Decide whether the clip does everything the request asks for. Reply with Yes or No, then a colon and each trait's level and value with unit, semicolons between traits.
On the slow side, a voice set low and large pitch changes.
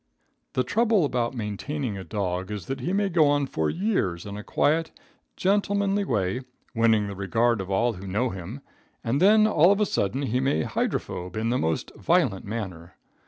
No: average, 185 wpm; low, 120 Hz; wide, 8.5 semitones